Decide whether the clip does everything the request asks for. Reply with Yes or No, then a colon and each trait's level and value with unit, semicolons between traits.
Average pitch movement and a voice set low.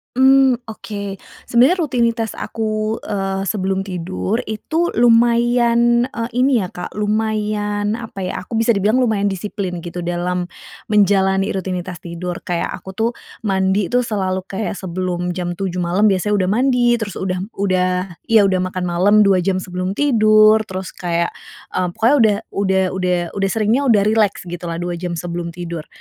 No: average, 3.4 semitones; high, 195 Hz